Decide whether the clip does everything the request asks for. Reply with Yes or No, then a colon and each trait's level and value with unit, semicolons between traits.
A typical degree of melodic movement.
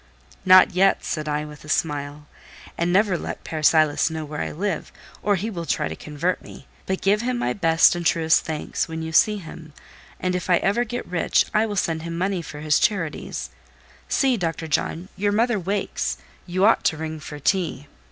Yes: average, 3.9 semitones